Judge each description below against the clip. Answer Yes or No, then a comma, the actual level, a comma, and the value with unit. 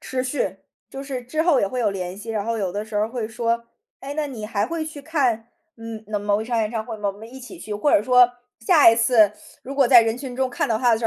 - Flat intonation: No, average, 3.2 semitones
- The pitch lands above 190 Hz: Yes, high, 230 Hz